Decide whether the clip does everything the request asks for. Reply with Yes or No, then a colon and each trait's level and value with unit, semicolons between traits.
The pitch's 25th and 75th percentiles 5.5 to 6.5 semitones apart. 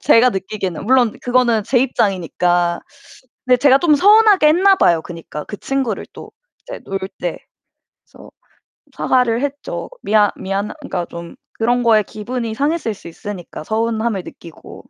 No: average, 5.1 semitones